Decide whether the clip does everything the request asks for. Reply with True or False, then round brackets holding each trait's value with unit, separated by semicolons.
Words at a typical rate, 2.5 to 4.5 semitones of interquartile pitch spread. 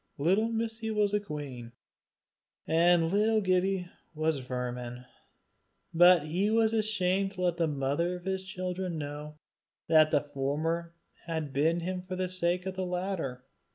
True (155 wpm; 3.9 semitones)